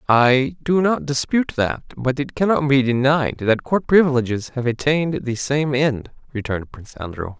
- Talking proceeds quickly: No, average, 170 wpm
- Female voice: No, male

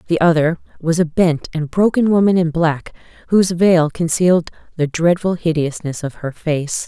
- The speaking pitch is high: No, medium, 165 Hz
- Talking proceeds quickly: No, average, 165 wpm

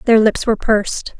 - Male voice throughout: No, female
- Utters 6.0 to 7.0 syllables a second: No, 5.8 syllables/s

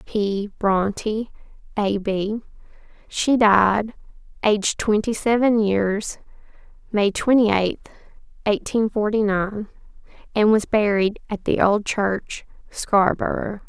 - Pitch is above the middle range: Yes, high, 210 Hz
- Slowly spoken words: Yes, slow, 105 wpm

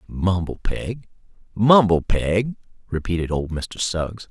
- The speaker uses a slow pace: Yes, slow, 110 wpm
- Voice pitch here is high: No, very low, 95 Hz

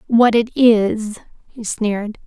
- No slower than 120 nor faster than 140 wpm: Yes, slow, 135 wpm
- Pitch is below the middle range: No, high, 220 Hz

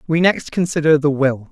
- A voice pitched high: No, medium, 150 Hz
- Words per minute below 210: Yes, average, 200 wpm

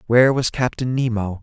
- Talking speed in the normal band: Yes, average, 170 wpm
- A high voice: No, low, 120 Hz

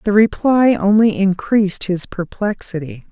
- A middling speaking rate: No, slow, 115 wpm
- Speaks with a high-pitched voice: Yes, high, 200 Hz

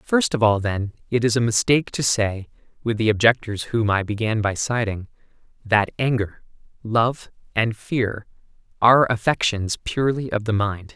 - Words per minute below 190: Yes, average, 160 wpm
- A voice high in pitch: No, low, 115 Hz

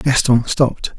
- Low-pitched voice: Yes, low, 130 Hz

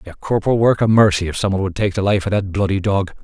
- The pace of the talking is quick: Yes, fast, 295 wpm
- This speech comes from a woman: No, male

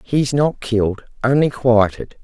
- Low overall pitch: Yes, low, 125 Hz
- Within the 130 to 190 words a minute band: Yes, slow, 135 wpm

